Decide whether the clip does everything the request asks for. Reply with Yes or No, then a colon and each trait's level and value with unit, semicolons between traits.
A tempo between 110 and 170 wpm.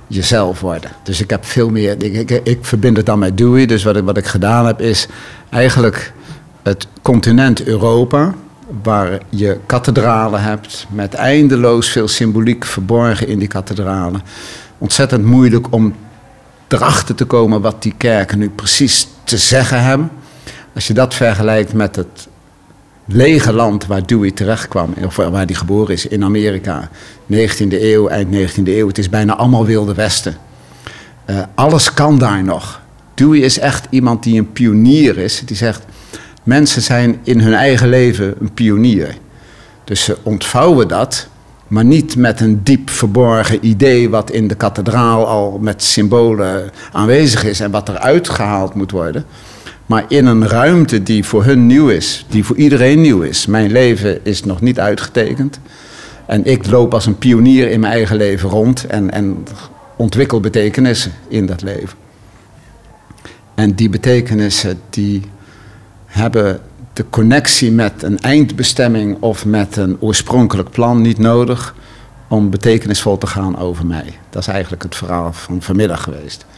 Yes: average, 155 wpm